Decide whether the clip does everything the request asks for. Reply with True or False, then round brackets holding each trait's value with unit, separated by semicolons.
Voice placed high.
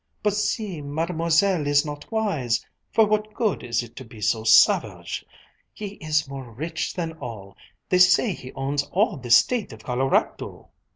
False (150 Hz)